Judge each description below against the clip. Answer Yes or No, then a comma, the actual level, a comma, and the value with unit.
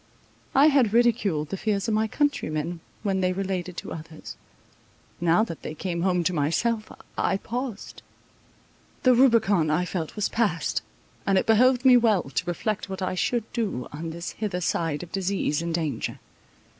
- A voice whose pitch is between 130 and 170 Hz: No, high, 190 Hz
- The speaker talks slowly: No, average, 170 wpm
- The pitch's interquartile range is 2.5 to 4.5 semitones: No, average, 5.0 semitones